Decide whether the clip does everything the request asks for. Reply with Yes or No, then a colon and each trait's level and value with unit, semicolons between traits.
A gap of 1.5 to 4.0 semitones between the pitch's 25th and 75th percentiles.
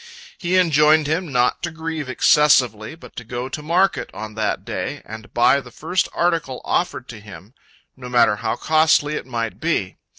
No: average, 5.2 semitones